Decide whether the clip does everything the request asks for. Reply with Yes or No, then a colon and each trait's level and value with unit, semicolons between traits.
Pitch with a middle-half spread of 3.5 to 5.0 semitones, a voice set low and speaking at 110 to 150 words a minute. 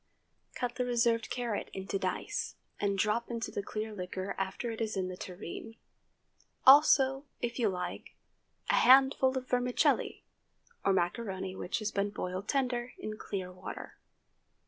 No: average, 4.4 semitones; high, 220 Hz; average, 145 wpm